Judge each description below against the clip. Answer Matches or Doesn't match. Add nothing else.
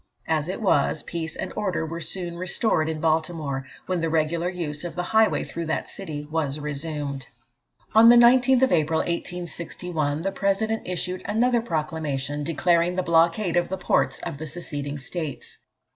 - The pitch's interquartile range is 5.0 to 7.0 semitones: Doesn't match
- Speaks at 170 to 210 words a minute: Doesn't match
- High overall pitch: Doesn't match